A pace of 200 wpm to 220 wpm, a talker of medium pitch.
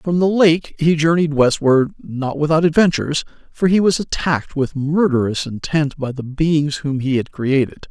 No: average, 175 wpm; medium, 150 Hz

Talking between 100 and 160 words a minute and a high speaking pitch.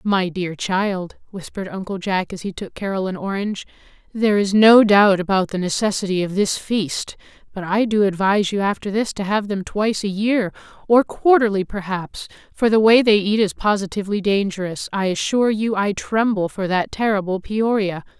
No: average, 180 wpm; high, 200 Hz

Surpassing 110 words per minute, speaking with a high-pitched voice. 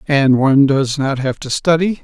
No: fast, 205 wpm; medium, 140 Hz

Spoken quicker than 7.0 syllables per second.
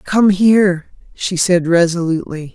No: 4.4 syllables/s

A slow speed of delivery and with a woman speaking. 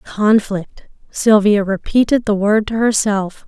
Yes: slow, 120 wpm; female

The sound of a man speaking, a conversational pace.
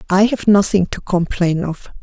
No: female; average, 180 wpm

